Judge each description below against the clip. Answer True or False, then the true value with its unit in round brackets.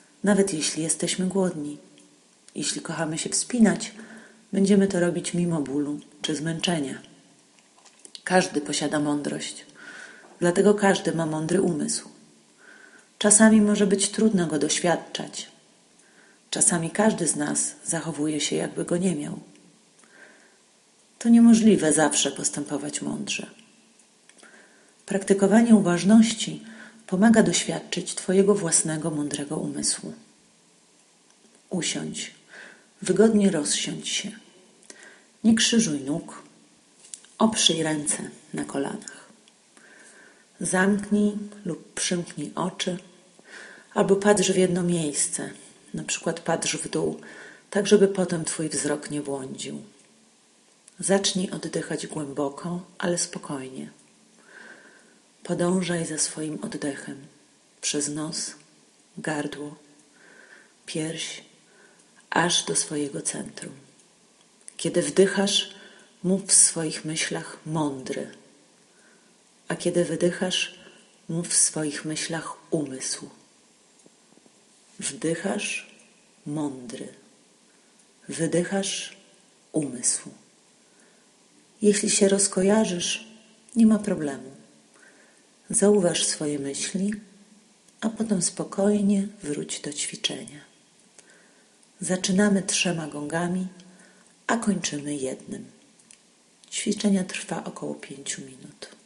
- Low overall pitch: False (180 Hz)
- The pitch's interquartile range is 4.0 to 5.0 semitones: True (4.6 semitones)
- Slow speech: True (90 wpm)